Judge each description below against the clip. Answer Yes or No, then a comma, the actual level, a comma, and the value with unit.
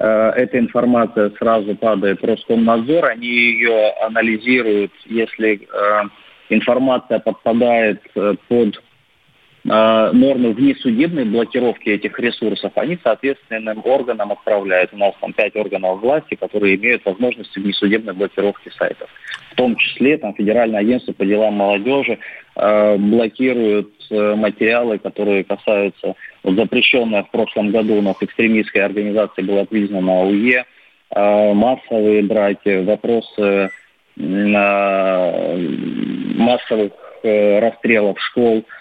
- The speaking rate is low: Yes, slow, 105 wpm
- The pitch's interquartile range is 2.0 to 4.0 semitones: Yes, narrow, 2.5 semitones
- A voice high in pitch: No, low, 110 Hz